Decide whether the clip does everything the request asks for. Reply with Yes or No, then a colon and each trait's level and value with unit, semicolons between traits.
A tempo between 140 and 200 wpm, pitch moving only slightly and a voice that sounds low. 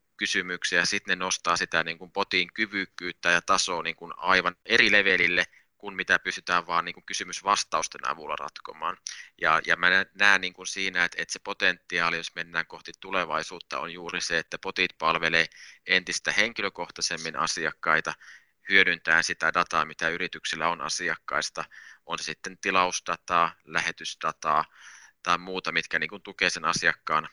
Yes: average, 150 wpm; narrow, 1.7 semitones; very low, 90 Hz